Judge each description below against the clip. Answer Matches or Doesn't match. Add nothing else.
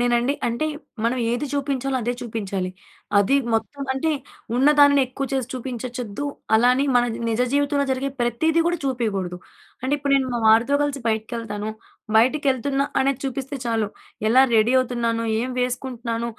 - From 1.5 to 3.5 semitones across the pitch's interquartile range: Matches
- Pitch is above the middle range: Matches